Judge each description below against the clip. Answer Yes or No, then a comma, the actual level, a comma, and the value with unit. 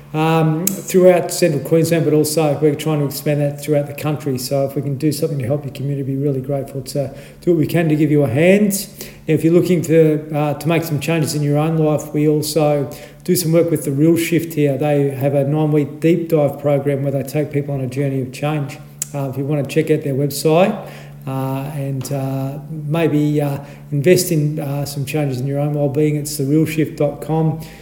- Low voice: No, medium, 150 Hz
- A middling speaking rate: No, fast, 220 wpm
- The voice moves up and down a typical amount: No, narrow, 2.0 semitones